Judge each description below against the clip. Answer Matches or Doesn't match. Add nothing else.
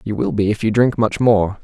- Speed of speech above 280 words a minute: Matches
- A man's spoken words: Matches